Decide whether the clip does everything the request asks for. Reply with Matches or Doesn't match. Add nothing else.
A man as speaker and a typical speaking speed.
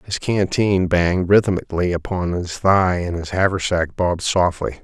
Matches